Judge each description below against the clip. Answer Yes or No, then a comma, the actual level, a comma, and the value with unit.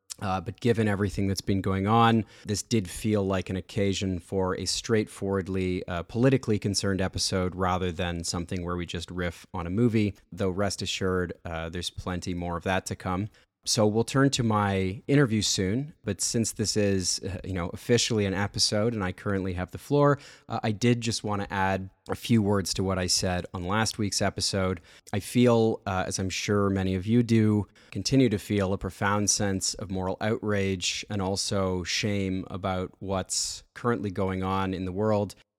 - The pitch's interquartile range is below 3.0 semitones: Yes, narrow, 2.5 semitones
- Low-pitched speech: Yes, low, 100 Hz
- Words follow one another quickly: No, average, 190 wpm